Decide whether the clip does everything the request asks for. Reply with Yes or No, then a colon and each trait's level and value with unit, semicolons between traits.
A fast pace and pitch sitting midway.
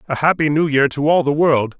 Yes: fast, 265 wpm; medium, 145 Hz